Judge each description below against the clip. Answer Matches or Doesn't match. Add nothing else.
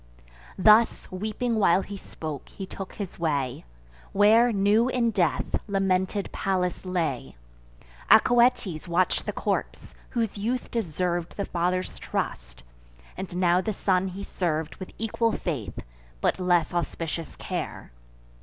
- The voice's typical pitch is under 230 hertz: Matches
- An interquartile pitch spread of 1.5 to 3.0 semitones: Doesn't match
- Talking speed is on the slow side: Matches